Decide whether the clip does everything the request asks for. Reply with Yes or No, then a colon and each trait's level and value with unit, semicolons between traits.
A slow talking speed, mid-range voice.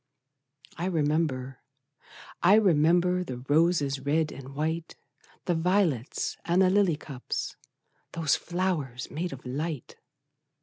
Yes: slow, 115 wpm; medium, 160 Hz